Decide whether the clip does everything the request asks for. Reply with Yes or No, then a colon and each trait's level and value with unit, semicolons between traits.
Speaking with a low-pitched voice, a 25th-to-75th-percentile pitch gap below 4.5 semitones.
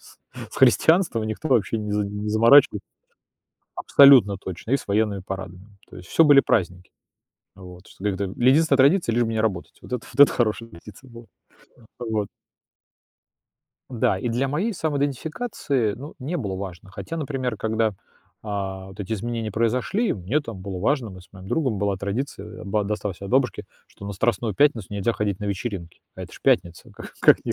No: low, 110 Hz; average, 5.0 semitones